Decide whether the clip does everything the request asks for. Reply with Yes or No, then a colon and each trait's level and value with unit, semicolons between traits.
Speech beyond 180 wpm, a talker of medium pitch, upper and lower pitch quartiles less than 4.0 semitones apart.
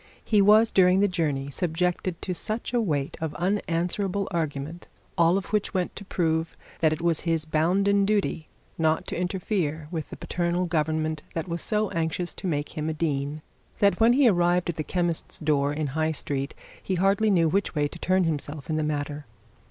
Yes: average, 190 wpm; medium, 170 Hz; average, 3.3 semitones